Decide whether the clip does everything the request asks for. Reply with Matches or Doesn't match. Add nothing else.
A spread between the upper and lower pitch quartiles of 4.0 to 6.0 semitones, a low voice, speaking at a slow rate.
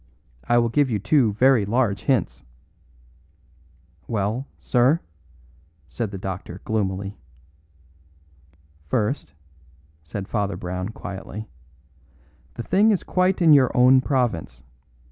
Matches